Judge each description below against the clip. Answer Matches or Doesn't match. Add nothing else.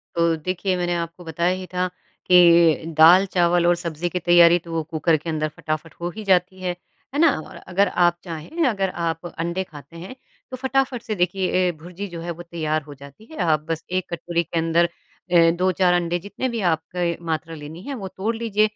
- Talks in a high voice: Doesn't match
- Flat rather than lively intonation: Matches